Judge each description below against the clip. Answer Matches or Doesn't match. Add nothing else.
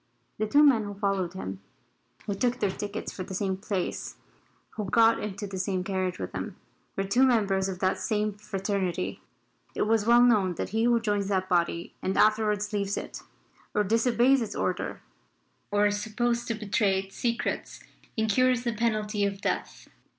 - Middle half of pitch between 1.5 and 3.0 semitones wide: Matches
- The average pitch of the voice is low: Doesn't match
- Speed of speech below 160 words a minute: Doesn't match